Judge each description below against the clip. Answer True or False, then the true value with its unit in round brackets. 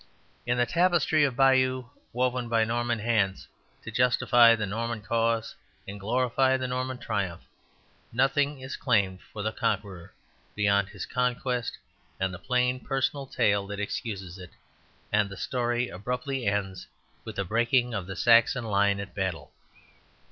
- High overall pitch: False (115 Hz)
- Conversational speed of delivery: True (150 wpm)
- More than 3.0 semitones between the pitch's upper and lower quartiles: True (3.9 semitones)